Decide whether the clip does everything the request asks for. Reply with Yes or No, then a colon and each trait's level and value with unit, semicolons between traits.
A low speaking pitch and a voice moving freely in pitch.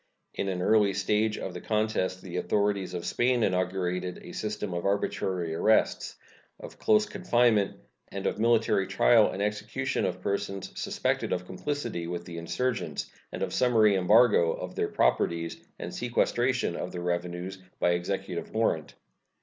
No: low, 100 Hz; average, 3.6 semitones